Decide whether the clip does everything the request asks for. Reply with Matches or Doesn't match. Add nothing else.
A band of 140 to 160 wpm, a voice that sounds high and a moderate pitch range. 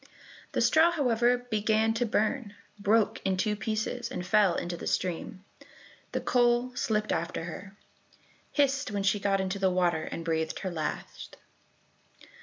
Matches